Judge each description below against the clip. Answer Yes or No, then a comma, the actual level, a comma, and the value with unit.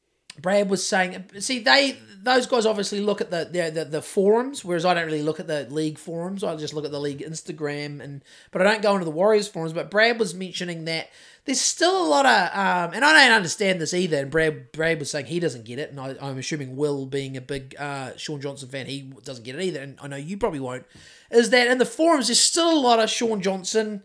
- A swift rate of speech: Yes, fast, 250 wpm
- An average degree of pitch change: No, wide, 6.9 semitones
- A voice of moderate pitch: Yes, medium, 175 Hz